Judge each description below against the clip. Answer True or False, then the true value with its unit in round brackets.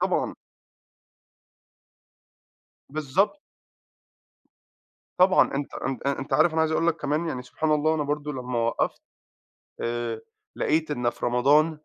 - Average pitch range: True (3.9 semitones)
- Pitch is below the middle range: False (150 Hz)